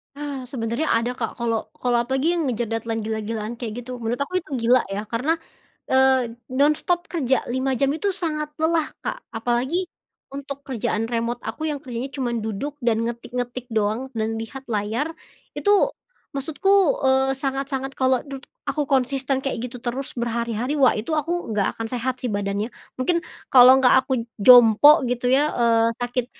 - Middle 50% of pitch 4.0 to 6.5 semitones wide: No, average, 3.3 semitones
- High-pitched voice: Yes, very high, 255 Hz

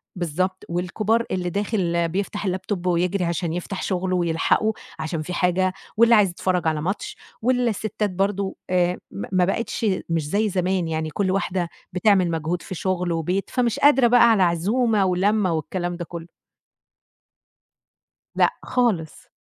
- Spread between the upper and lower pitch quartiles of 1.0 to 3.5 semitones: Yes, average, 3.1 semitones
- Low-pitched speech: No, medium, 185 Hz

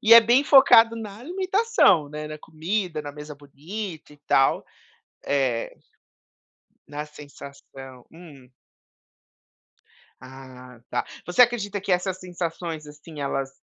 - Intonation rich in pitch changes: Yes, wide, 6.3 semitones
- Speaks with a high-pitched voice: No, medium, 160 Hz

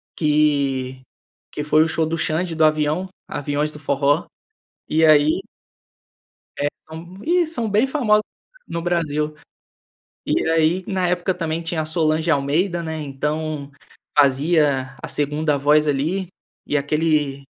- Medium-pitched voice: Yes, medium, 155 Hz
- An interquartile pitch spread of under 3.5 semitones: Yes, narrow, 2.5 semitones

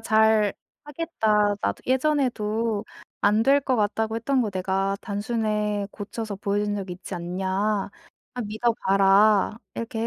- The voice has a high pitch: Yes, high, 210 Hz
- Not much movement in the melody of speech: Yes, narrow, 2.3 semitones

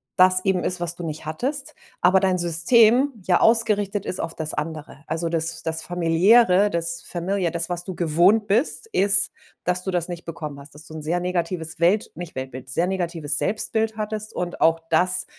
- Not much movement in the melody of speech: No, average, 3.2 semitones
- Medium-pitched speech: Yes, medium, 175 Hz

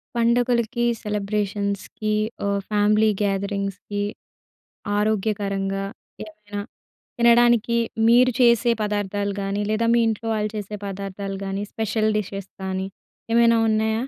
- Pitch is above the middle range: Yes, high, 210 Hz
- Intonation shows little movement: Yes, narrow, 2.2 semitones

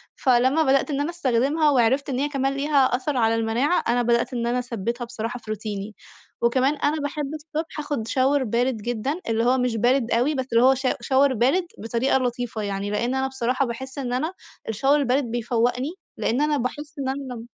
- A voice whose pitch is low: No, very high, 255 Hz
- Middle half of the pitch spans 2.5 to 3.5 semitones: Yes, average, 3.0 semitones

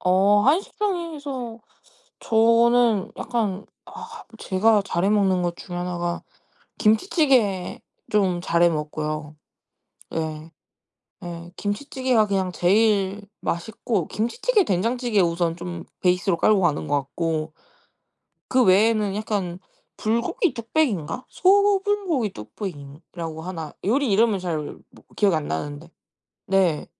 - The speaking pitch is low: No, high, 195 Hz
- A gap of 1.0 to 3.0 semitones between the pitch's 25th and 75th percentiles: No, average, 5.3 semitones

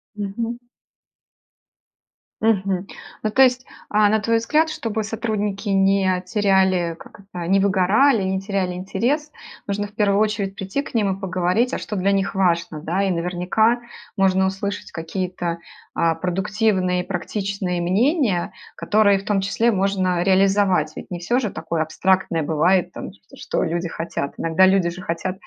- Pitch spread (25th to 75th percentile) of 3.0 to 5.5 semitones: No, narrow, 2.6 semitones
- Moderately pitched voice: No, high, 195 Hz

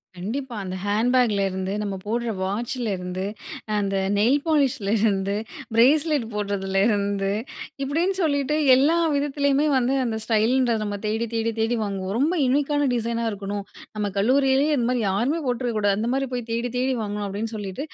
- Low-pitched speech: No, high, 230 Hz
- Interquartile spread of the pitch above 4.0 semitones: Yes, average, 4.7 semitones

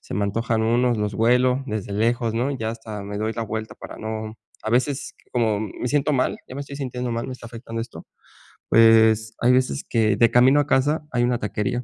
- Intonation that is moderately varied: No, narrow, 2.3 semitones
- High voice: No, low, 115 Hz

